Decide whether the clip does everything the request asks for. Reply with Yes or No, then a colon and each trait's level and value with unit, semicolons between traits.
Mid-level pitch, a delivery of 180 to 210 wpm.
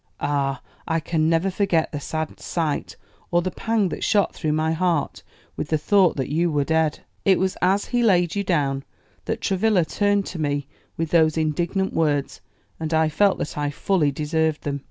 Yes: medium, 160 Hz; average, 190 wpm